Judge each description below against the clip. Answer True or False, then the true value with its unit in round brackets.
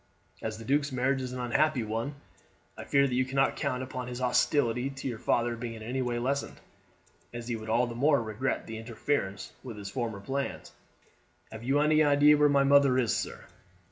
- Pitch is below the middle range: True (125 Hz)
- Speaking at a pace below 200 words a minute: False (205 wpm)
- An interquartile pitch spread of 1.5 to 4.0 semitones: True (3.1 semitones)